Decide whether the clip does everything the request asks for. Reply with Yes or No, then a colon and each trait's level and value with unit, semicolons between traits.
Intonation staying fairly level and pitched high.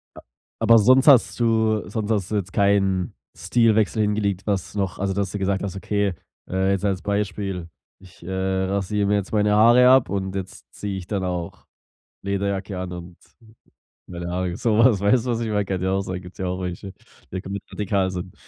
No: narrow, 2.0 semitones; low, 100 Hz